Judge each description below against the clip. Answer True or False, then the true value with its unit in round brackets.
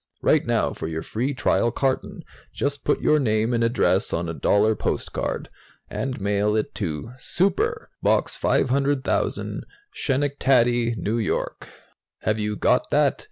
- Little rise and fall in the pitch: False (4.5 semitones)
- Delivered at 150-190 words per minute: False (140 wpm)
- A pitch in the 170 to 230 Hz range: False (115 Hz)